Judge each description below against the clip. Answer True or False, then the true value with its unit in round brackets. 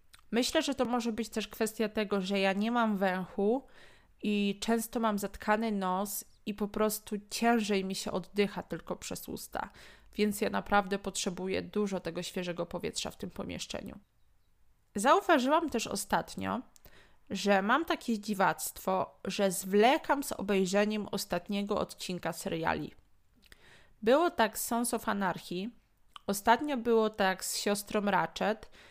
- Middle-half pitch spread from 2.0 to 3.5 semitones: True (2.7 semitones)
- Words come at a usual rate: True (135 wpm)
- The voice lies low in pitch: False (210 Hz)